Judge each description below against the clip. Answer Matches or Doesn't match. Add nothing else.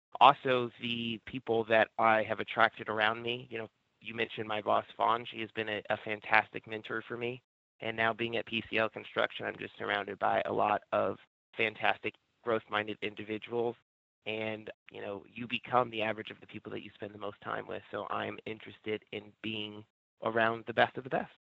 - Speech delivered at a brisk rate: Doesn't match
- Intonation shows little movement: Matches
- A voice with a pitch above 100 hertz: Matches